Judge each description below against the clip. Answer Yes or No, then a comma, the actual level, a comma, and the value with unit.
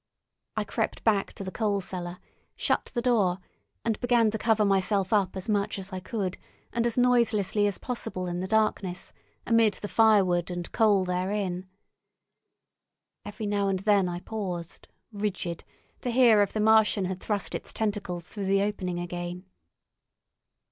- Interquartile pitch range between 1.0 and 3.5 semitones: Yes, average, 3.1 semitones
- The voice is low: No, high, 200 Hz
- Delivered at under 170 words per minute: Yes, average, 160 wpm